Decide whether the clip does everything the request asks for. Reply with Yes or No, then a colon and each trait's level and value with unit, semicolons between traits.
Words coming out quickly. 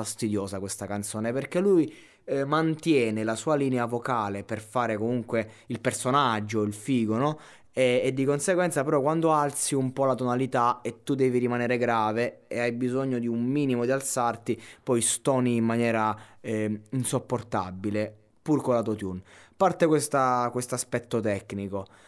No: average, 160 wpm